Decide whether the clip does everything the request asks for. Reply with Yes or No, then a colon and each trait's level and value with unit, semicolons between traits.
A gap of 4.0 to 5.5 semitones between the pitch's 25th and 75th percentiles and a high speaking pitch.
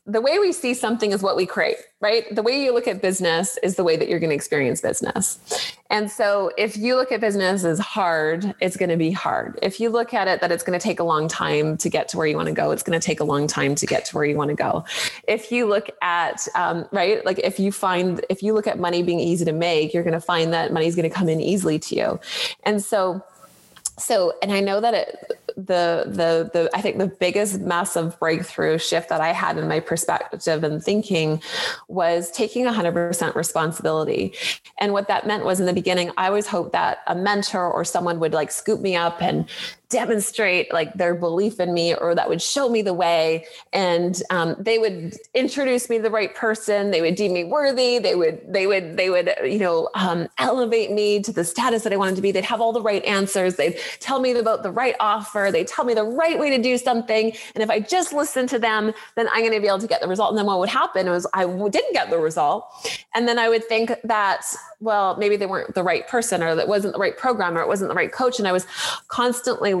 Yes: average, 4.6 semitones; high, 200 Hz